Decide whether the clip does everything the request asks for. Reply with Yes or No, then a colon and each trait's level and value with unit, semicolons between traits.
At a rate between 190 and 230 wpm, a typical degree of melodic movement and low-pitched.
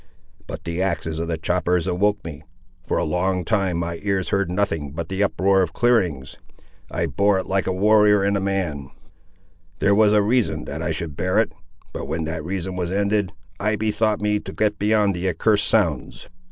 Yes: average, 195 wpm; average, 3.6 semitones; very low, 95 Hz